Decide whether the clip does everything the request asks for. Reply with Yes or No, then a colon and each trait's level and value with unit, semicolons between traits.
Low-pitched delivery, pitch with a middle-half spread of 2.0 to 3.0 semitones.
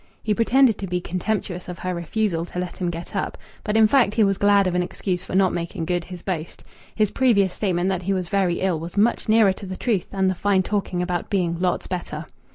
No: medium, 185 Hz; narrow, 2.4 semitones